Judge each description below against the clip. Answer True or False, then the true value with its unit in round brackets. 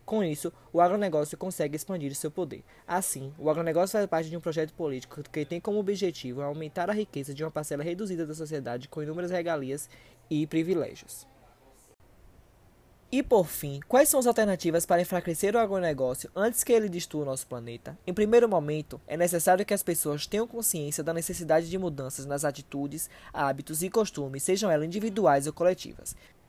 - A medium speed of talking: True (175 wpm)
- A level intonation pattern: False (4.2 semitones)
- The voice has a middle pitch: True (165 Hz)